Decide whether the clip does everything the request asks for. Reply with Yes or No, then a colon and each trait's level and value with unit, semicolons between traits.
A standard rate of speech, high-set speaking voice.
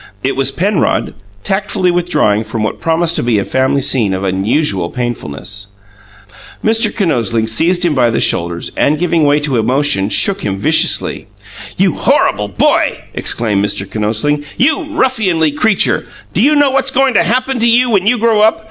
No: average, 170 wpm; medium, 150 Hz